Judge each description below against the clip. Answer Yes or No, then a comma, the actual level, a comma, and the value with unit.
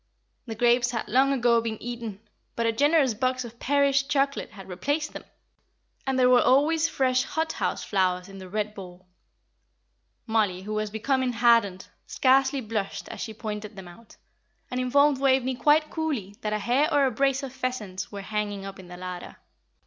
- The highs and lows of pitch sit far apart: No, average, 4.6 semitones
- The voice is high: Yes, high, 235 Hz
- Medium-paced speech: Yes, average, 180 wpm